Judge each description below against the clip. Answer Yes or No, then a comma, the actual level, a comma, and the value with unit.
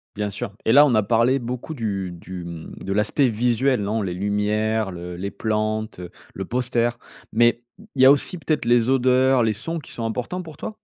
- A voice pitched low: Yes, low, 115 Hz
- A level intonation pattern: No, average, 3.8 semitones